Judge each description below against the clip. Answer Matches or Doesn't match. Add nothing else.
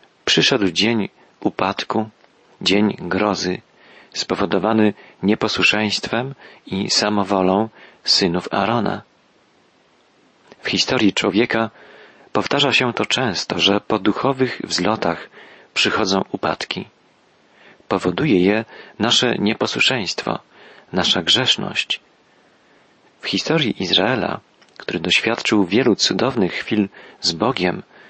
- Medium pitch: Doesn't match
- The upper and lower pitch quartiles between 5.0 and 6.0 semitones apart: Doesn't match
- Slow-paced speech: Matches